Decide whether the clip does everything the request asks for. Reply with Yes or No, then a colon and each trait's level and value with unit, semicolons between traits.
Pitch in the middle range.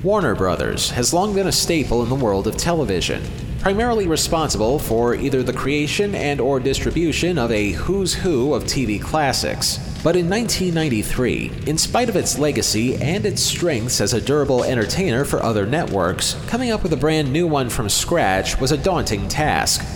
Yes: medium, 145 Hz